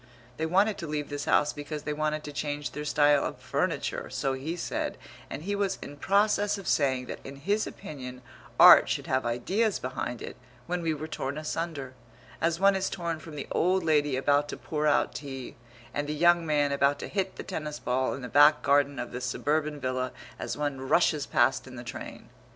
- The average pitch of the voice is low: No, medium, 150 Hz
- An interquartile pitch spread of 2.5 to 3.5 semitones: Yes, average, 3.2 semitones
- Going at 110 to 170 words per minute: No, fast, 205 wpm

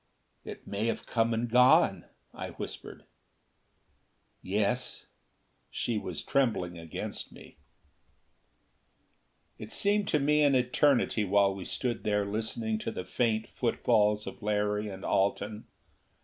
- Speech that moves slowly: Yes, slow, 120 wpm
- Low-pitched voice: Yes, low, 110 Hz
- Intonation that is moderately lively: Yes, average, 3.2 semitones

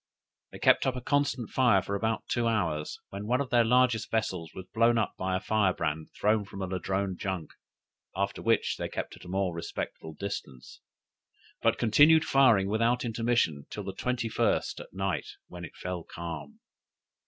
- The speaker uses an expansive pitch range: No, average, 4.4 semitones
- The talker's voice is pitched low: Yes, low, 100 Hz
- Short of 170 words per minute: No, average, 175 wpm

